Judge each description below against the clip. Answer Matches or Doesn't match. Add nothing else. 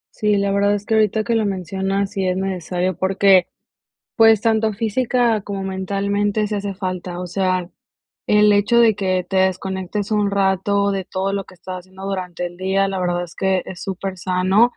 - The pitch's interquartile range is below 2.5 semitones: Matches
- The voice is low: Doesn't match